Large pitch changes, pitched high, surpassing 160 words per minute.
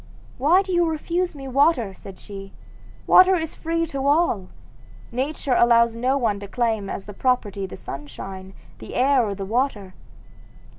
No: wide, 7.2 semitones; high, 245 Hz; average, 155 wpm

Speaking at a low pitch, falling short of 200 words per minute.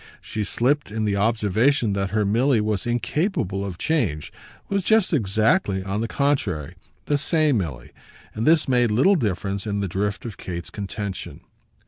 Yes: low, 110 Hz; average, 160 wpm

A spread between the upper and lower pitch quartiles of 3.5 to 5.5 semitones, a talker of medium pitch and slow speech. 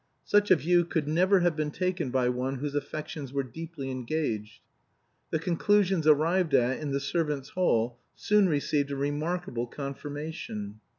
No: average, 4.4 semitones; medium, 150 Hz; average, 155 wpm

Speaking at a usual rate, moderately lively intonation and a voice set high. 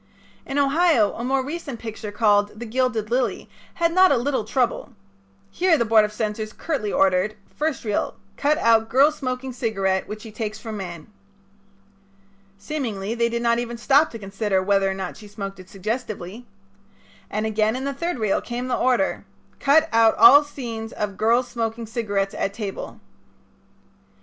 Yes: average, 170 wpm; average, 3.8 semitones; high, 230 Hz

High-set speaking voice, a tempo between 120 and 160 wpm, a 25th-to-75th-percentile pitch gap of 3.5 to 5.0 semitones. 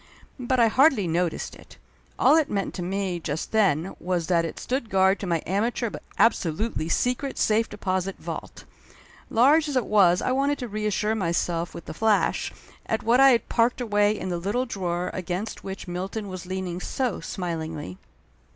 No: high, 195 Hz; average, 180 wpm; average, 4.6 semitones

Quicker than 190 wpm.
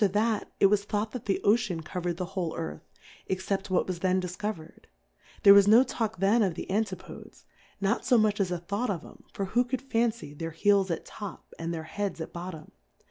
Yes: average, 200 wpm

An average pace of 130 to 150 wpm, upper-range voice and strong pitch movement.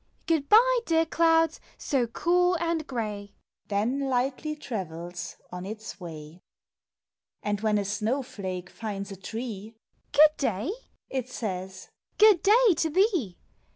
Yes: average, 140 wpm; high, 240 Hz; wide, 8.4 semitones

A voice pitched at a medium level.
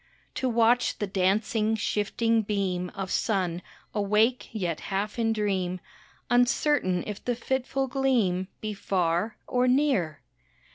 No: high, 210 Hz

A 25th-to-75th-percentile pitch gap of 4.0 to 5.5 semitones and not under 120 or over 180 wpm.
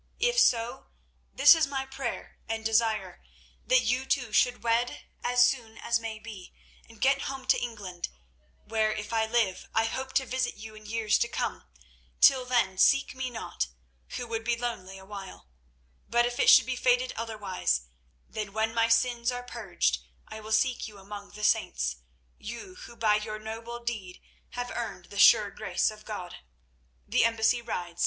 No: narrow, 2.5 semitones; average, 175 wpm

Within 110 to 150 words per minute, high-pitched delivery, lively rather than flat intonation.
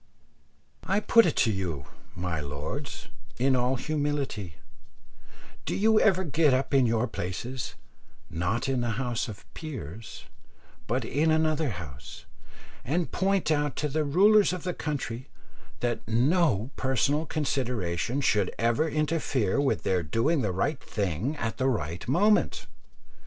No: average, 140 wpm; low, 130 Hz; wide, 6.4 semitones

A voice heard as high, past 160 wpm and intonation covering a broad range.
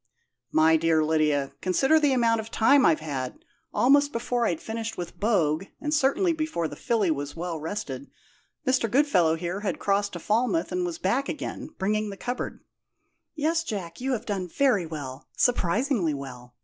Yes: high, 200 Hz; average, 175 wpm; wide, 7.5 semitones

